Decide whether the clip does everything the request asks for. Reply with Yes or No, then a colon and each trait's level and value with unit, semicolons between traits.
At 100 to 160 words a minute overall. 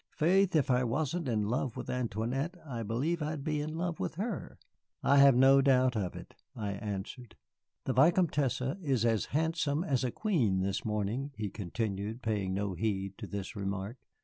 No: average, 175 wpm